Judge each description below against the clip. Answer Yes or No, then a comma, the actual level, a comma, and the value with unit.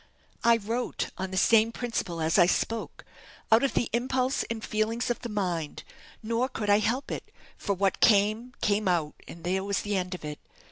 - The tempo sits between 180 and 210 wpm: Yes, average, 195 wpm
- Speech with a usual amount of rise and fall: Yes, average, 3.7 semitones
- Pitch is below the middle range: No, high, 210 Hz